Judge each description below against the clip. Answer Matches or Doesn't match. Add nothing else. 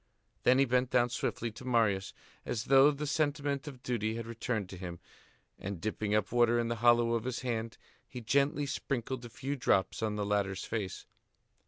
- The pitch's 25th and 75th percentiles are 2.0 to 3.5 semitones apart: Matches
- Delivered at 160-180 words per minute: Doesn't match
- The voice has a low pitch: Matches